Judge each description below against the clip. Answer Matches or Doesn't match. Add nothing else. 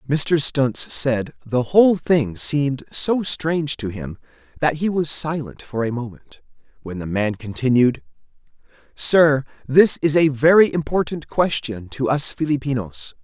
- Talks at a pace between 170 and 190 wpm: Doesn't match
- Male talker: Matches